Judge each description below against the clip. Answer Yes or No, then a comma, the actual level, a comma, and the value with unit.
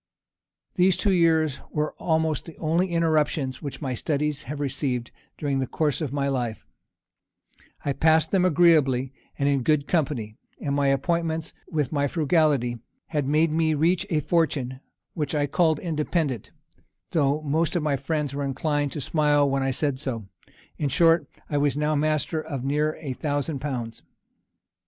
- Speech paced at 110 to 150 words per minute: No, average, 160 wpm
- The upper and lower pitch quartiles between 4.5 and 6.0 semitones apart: No, narrow, 2.5 semitones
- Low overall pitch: No, medium, 150 Hz